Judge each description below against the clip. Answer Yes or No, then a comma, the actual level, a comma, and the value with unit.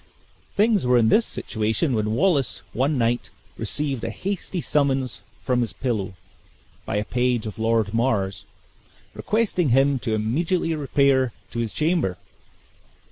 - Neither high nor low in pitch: No, low, 125 Hz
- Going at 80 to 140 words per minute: Yes, slow, 135 wpm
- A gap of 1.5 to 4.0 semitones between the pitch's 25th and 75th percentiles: No, average, 5.2 semitones